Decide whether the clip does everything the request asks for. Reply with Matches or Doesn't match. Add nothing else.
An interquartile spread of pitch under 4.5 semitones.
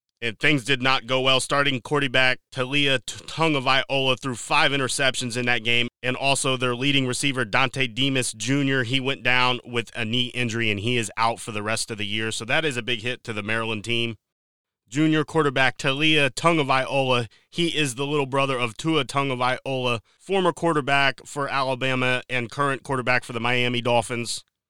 Matches